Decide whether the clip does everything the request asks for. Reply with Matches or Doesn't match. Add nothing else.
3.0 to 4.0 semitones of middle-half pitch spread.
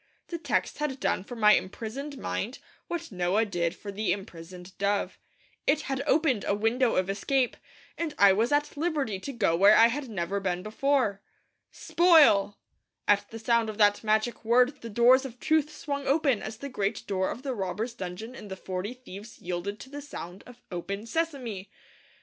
Doesn't match